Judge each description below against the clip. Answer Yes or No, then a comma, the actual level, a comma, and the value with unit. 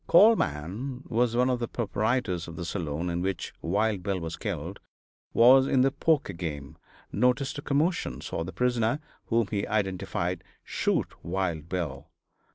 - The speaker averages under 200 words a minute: Yes, average, 160 wpm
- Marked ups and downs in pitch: Yes, wide, 6.5 semitones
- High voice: No, low, 105 Hz